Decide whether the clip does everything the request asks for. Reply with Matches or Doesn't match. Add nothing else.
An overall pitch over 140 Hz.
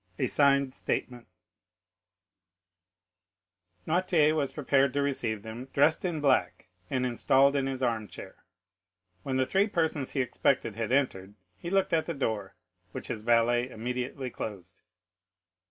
Doesn't match